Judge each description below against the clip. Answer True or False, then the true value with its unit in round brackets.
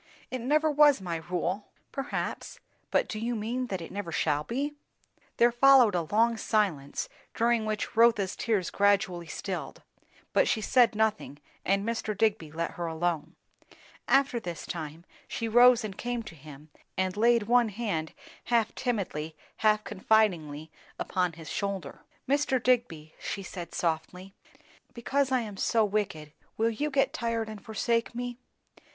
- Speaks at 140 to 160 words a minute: True (150 wpm)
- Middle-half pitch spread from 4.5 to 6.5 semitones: True (5.4 semitones)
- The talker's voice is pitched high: True (215 Hz)